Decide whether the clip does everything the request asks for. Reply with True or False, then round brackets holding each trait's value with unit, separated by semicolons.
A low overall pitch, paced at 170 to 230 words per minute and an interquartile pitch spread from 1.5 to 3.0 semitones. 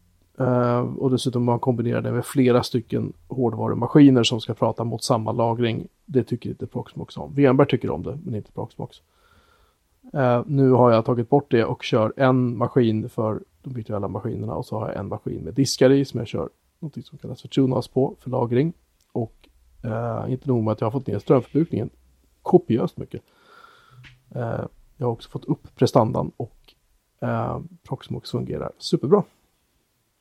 True (125 Hz; 180 wpm; 2.6 semitones)